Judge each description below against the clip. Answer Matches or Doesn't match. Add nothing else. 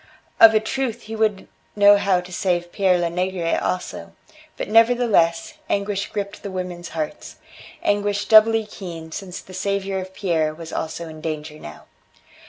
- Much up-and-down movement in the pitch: Doesn't match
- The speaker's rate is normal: Matches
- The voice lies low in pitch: Doesn't match